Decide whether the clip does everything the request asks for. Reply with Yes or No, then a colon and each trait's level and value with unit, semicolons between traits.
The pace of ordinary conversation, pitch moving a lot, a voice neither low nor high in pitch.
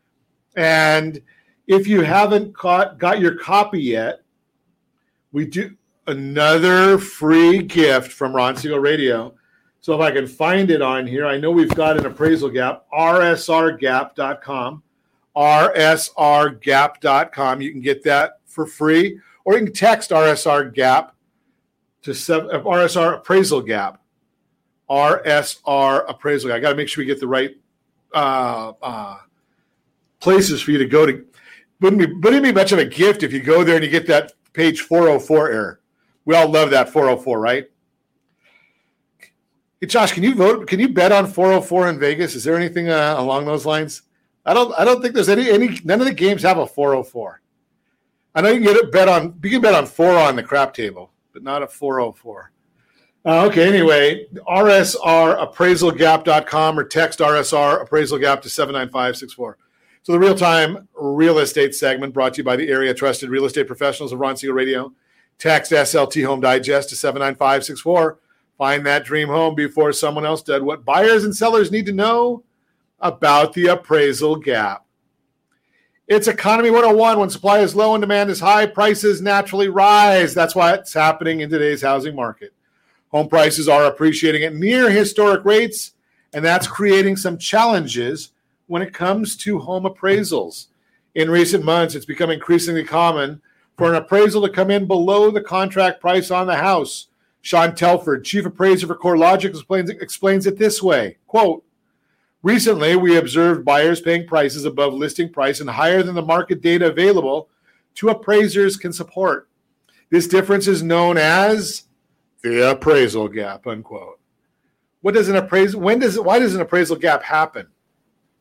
No: average, 160 wpm; average, 4.9 semitones; medium, 165 Hz